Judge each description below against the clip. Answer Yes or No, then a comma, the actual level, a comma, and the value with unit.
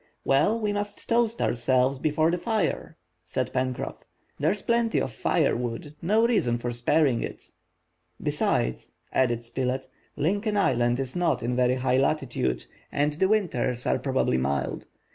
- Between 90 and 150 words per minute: Yes, average, 145 wpm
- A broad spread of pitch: Yes, wide, 7.9 semitones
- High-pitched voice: No, low, 135 Hz